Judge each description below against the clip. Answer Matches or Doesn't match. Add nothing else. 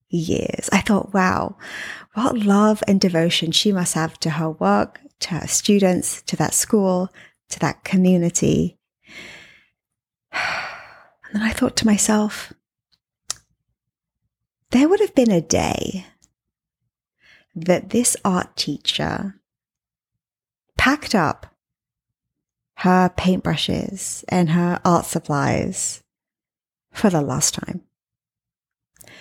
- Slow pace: Matches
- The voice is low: Doesn't match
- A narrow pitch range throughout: Doesn't match